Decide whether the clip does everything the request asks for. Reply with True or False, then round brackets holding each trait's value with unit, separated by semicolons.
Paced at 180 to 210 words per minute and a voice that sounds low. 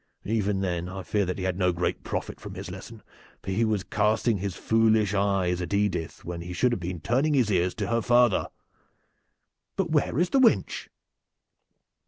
True (190 wpm; 100 Hz)